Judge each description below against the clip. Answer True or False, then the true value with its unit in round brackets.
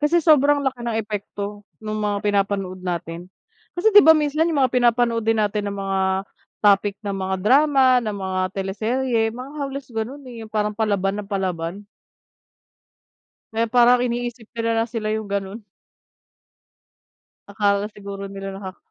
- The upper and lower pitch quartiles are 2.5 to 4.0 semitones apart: True (3.6 semitones)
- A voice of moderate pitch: False (215 Hz)